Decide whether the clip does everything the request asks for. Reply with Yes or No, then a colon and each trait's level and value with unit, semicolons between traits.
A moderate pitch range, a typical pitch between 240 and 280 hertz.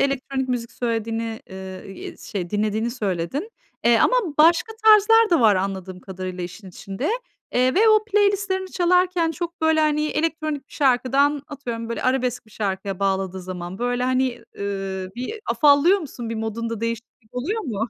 No: wide, 7.4 semitones; high, 245 Hz